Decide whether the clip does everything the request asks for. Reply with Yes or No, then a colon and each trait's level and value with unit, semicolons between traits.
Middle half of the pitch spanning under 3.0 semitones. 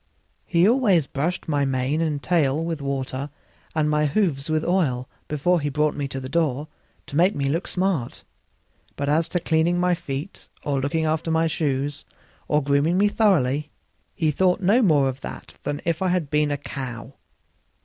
No: average, 3.6 semitones